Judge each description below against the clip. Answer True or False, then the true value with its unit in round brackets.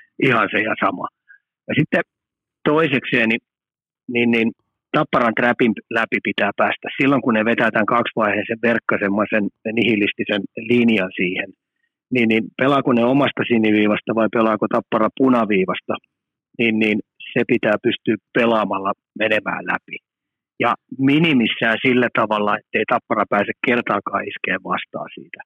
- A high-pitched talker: False (115 Hz)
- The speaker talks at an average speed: True (125 wpm)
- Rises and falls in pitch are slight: True (2.3 semitones)